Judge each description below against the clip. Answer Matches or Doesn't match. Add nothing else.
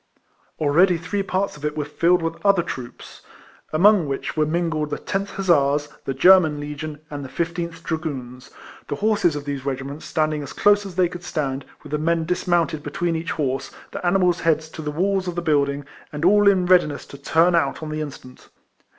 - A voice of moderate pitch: Matches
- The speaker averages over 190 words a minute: Matches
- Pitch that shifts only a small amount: Doesn't match